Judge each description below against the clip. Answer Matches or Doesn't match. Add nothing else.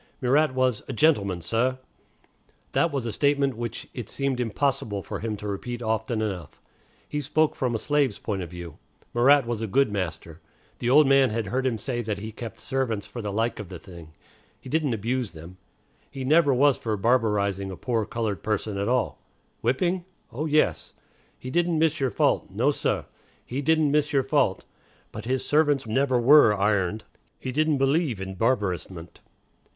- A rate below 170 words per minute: Doesn't match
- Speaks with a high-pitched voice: Doesn't match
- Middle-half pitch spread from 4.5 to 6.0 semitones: Matches